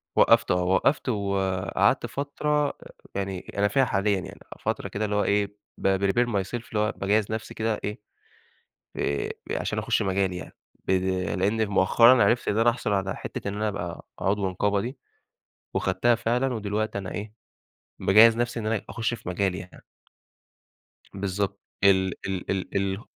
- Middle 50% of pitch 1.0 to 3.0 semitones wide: Yes, average, 2.7 semitones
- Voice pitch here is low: Yes, low, 100 Hz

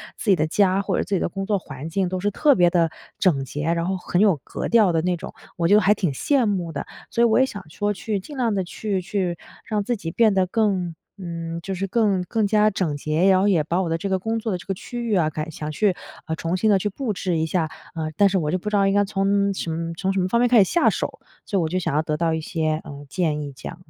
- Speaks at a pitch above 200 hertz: No, medium, 185 Hz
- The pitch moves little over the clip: No, average, 3.7 semitones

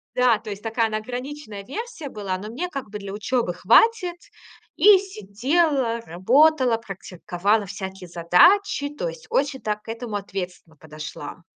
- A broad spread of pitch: Yes, wide, 6.6 semitones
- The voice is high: Yes, high, 225 Hz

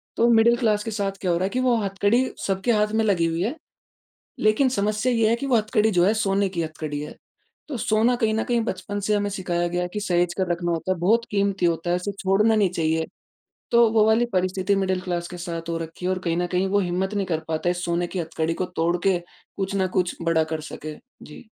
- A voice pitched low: No, high, 190 Hz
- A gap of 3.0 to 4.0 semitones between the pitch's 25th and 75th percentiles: Yes, average, 3.6 semitones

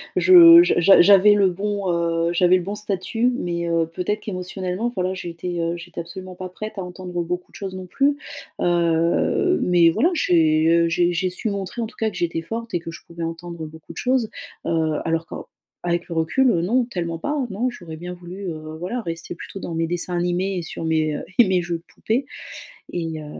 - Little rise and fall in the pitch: No, average, 3.1 semitones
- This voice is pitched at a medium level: Yes, medium, 180 Hz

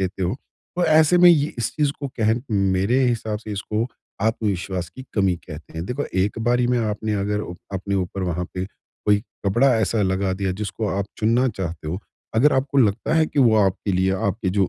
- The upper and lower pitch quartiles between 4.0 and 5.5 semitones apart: Yes, average, 4.3 semitones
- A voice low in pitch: Yes, low, 105 Hz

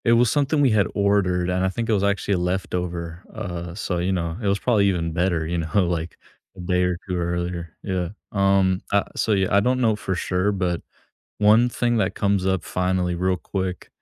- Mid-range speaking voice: No, very low, 95 Hz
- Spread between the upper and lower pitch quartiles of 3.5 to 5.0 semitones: No, narrow, 2.5 semitones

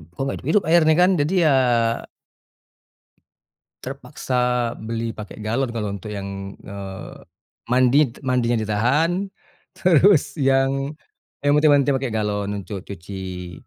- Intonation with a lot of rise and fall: Yes, wide, 5.7 semitones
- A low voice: Yes, low, 125 Hz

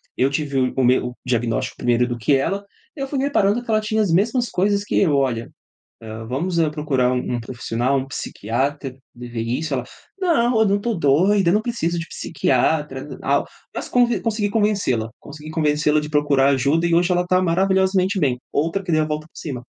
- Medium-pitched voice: Yes, medium, 155 Hz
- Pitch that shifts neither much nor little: No, wide, 7.1 semitones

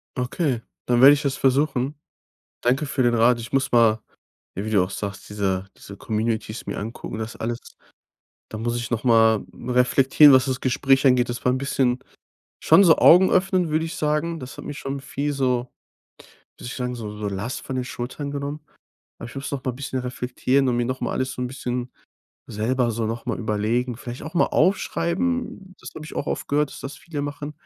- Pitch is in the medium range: No, low, 125 Hz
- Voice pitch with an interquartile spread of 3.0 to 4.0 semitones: Yes, average, 3.3 semitones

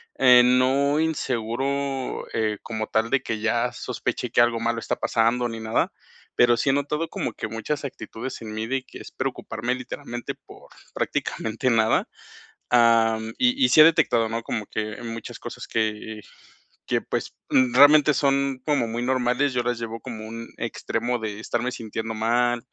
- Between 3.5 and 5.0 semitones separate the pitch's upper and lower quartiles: No, average, 2.9 semitones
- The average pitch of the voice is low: Yes, low, 120 Hz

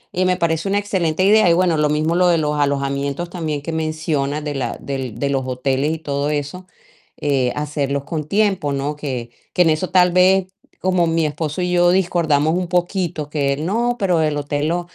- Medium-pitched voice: Yes, medium, 155 Hz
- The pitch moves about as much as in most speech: Yes, average, 3.8 semitones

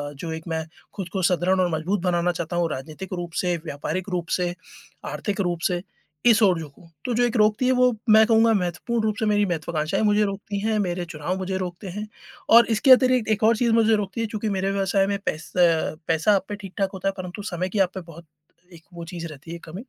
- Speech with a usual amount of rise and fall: Yes, average, 3.5 semitones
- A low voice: No, high, 190 Hz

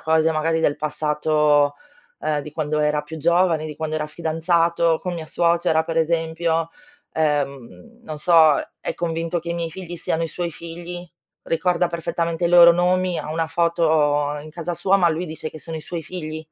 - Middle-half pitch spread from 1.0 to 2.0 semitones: Yes, narrow, 1.7 semitones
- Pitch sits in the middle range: Yes, medium, 165 Hz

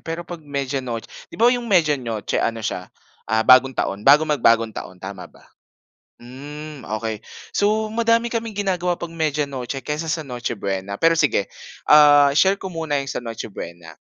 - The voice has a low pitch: No, medium, 145 Hz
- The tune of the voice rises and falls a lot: Yes, wide, 6.3 semitones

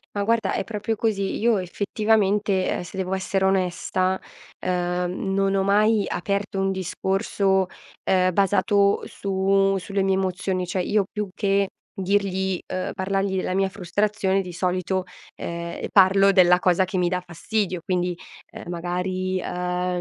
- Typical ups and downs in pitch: No, narrow, 1.5 semitones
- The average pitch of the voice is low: No, high, 190 Hz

